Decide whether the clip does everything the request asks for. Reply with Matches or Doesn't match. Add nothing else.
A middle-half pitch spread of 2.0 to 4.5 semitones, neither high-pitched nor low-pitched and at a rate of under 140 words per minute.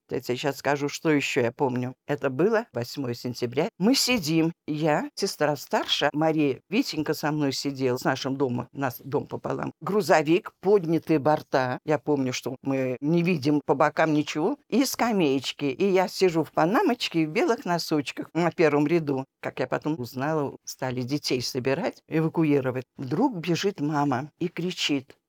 Doesn't match